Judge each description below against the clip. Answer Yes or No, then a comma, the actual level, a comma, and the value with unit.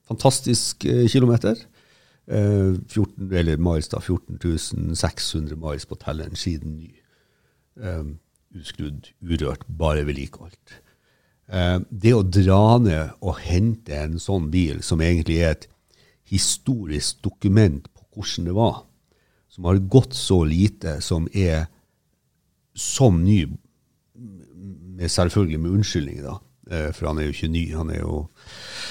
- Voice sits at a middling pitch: No, very low, 90 Hz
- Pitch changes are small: No, average, 4.7 semitones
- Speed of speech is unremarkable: No, slow, 125 wpm